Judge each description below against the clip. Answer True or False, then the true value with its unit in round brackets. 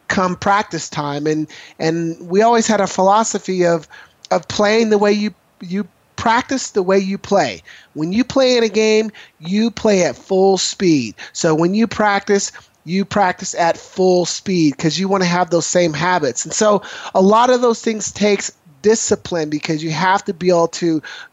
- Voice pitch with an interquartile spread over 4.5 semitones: False (3.7 semitones)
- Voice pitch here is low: False (195 Hz)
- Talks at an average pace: True (185 wpm)